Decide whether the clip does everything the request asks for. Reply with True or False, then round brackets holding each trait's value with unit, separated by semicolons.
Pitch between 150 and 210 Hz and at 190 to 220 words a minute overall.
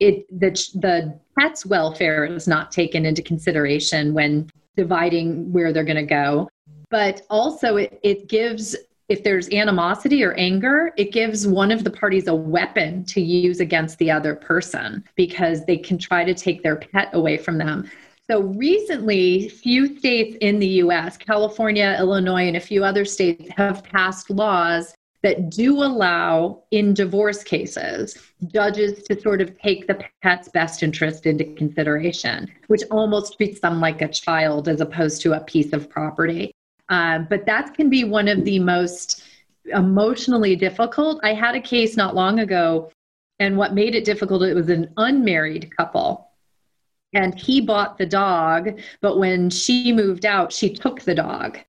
False (190 Hz; 165 wpm)